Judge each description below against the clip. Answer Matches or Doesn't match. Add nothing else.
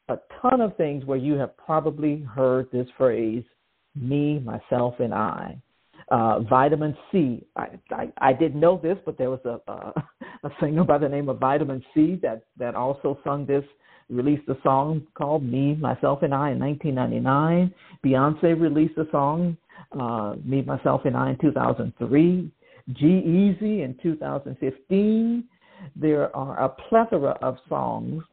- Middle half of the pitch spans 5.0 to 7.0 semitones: Doesn't match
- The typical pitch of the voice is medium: Matches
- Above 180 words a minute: Doesn't match